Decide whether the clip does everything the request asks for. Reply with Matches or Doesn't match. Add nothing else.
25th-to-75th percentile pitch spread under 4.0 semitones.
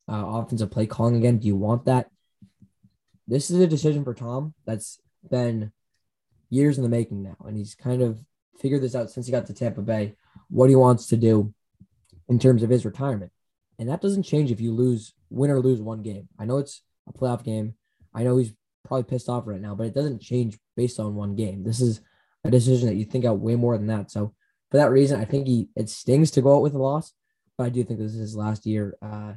Matches